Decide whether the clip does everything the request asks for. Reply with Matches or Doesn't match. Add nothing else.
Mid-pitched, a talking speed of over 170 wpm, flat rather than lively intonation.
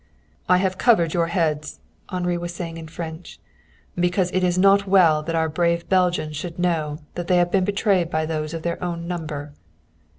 Matches